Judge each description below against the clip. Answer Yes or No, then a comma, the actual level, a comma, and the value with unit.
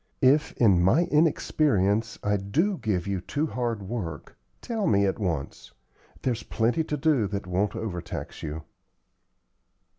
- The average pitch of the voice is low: Yes, low, 105 Hz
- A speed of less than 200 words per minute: Yes, average, 140 wpm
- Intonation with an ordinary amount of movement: No, wide, 7.0 semitones